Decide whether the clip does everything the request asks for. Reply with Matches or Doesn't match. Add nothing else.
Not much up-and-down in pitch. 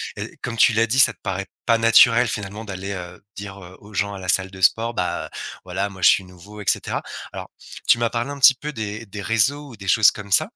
Doesn't match